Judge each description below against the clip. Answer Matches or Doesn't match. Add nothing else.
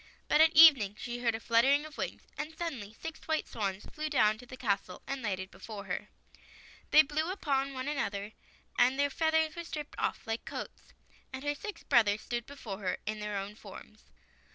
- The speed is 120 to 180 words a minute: Doesn't match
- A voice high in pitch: Matches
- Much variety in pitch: Matches